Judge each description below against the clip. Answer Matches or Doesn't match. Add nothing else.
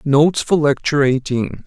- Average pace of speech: Matches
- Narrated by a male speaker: Matches